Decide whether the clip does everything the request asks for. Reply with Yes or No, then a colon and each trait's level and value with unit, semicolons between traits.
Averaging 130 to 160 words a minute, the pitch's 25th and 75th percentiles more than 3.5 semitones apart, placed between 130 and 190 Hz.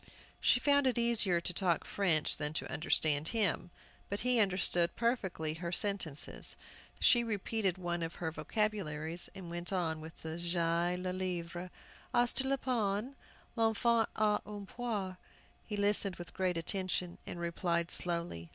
Yes: average, 150 wpm; average, 3.9 semitones; medium, 185 Hz